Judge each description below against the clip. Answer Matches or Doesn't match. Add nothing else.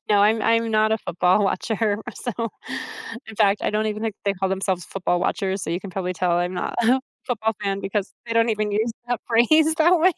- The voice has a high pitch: Matches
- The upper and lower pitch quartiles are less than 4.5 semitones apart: Matches